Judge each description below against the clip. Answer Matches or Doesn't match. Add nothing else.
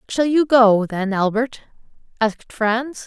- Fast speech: Doesn't match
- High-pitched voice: Matches